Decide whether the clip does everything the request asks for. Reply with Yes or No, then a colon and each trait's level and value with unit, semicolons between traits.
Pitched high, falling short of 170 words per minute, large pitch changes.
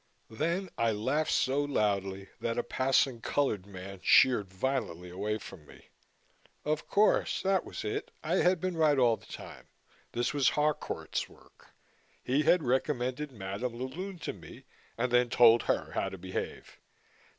No: low, 125 Hz; average, 160 wpm; wide, 6.2 semitones